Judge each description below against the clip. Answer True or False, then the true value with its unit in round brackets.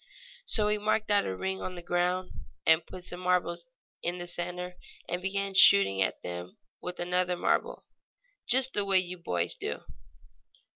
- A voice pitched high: False (180 Hz)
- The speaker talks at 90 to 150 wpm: False (160 wpm)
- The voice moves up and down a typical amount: False (1.7 semitones)